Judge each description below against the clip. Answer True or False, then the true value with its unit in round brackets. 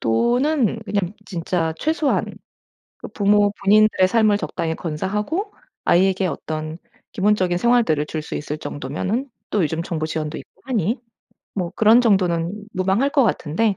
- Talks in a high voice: True (195 Hz)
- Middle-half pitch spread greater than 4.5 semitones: True (5.3 semitones)